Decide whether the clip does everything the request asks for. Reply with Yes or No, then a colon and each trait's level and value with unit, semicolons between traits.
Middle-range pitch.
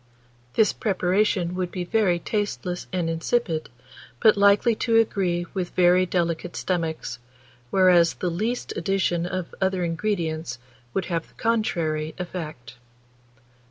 Yes: medium, 180 Hz